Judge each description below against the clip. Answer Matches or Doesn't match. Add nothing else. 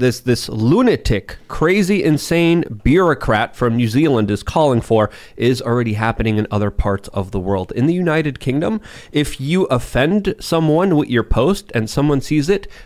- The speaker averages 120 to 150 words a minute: Doesn't match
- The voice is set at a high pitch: Doesn't match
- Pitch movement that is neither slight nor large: Doesn't match